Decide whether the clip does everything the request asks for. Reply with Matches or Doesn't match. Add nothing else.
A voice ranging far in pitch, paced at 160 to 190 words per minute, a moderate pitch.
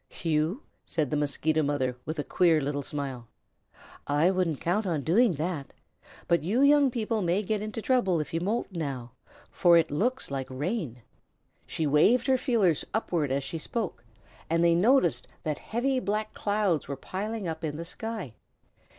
Matches